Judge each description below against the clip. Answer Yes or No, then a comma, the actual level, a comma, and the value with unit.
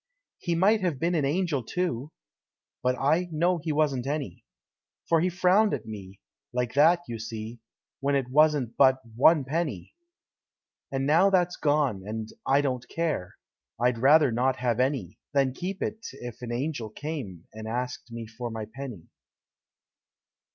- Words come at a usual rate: Yes, average, 160 wpm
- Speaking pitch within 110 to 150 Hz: Yes, low, 135 Hz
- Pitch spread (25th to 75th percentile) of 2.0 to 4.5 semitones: No, average, 5.1 semitones